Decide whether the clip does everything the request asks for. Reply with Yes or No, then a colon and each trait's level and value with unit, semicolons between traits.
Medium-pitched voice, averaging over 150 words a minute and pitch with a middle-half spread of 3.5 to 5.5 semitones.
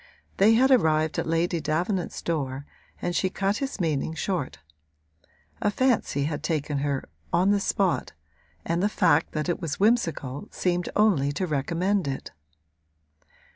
No: medium, 170 Hz; average, 145 wpm; average, 4.6 semitones